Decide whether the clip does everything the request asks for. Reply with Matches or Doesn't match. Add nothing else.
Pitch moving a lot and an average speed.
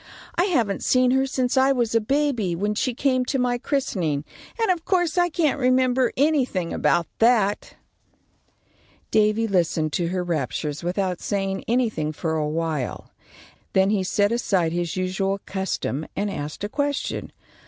Matches